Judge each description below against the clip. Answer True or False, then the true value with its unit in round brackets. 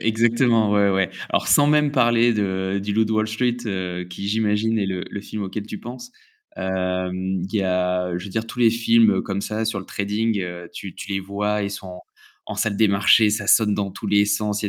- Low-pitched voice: True (105 Hz)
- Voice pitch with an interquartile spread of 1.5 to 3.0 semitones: True (2.7 semitones)